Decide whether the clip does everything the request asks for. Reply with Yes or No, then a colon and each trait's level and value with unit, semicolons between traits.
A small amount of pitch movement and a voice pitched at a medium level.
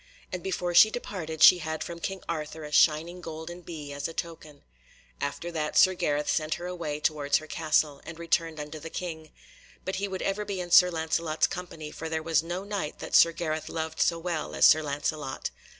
Yes: narrow, 2.3 semitones; medium, 160 Hz